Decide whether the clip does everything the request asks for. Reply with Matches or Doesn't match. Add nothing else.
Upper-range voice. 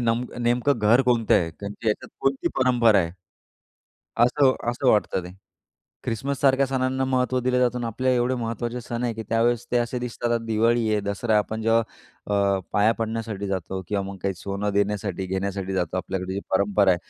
Doesn't match